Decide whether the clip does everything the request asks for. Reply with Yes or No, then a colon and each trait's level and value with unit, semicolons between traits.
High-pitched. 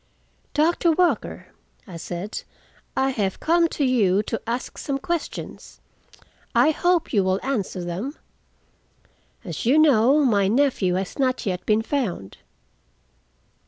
Yes: high, 245 Hz